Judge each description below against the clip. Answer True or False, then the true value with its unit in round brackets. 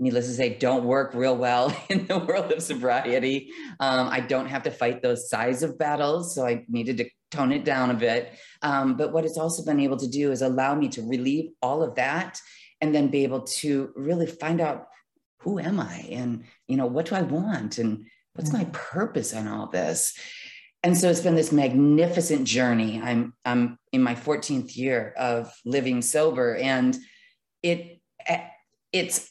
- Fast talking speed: False (190 wpm)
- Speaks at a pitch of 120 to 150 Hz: True (135 Hz)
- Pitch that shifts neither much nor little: True (4.2 semitones)